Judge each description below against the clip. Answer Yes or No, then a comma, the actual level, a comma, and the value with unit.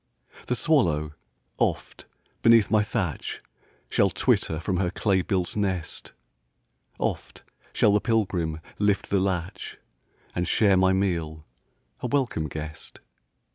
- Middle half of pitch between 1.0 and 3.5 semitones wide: No, average, 4.0 semitones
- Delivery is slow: Yes, slow, 120 wpm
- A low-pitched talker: Yes, very low, 95 Hz